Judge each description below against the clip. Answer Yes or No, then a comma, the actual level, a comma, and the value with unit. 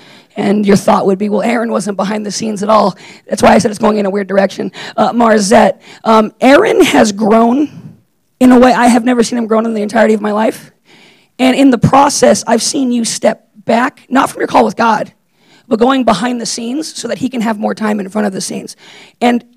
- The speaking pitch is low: No, high, 225 Hz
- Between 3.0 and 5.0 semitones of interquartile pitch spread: No, narrow, 2.5 semitones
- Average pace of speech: No, fast, 235 wpm